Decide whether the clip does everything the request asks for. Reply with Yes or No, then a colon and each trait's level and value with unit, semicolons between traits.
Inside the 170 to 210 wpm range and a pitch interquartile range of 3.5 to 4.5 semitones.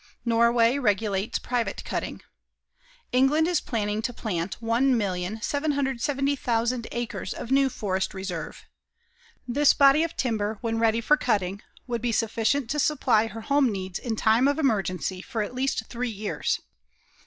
No: average, 140 wpm; average, 4.2 semitones